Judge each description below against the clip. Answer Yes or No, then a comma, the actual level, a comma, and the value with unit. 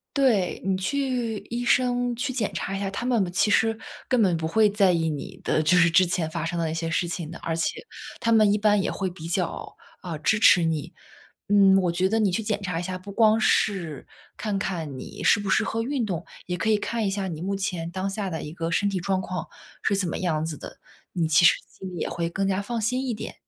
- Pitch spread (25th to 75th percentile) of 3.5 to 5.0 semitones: Yes, average, 4.2 semitones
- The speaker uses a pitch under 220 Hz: Yes, high, 190 Hz